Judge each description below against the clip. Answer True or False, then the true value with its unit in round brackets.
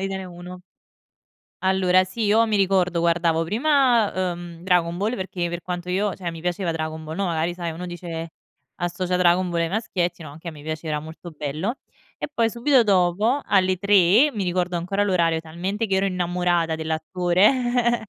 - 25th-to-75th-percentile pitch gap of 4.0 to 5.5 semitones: False (2.7 semitones)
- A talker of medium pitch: True (180 Hz)